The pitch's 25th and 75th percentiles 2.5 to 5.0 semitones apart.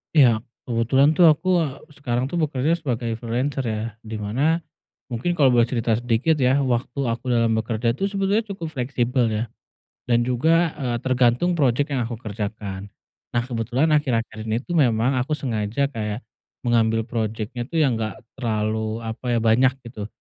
Yes: average, 3.8 semitones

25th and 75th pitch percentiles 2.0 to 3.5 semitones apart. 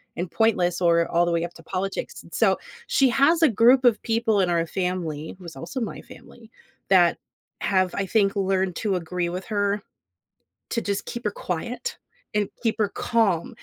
No: average, 4.4 semitones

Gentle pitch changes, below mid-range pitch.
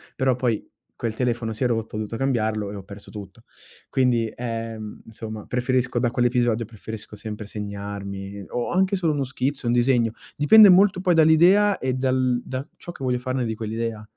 No: average, 3.3 semitones; low, 120 Hz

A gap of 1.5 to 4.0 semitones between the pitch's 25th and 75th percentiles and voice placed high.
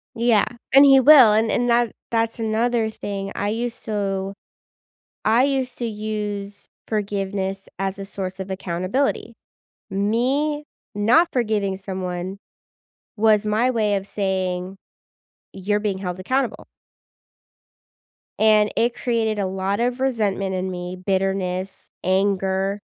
Yes: average, 3.2 semitones; high, 205 Hz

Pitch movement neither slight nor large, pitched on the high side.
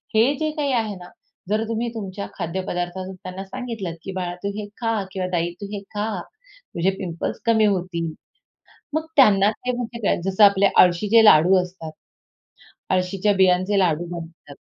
Yes: average, 3.4 semitones; high, 195 Hz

